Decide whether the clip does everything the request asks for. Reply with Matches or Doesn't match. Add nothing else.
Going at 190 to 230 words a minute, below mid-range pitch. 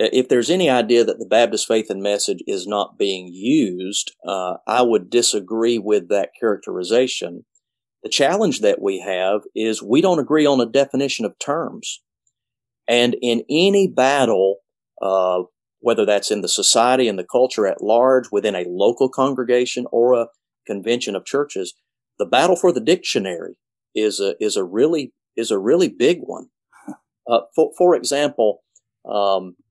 Doesn't match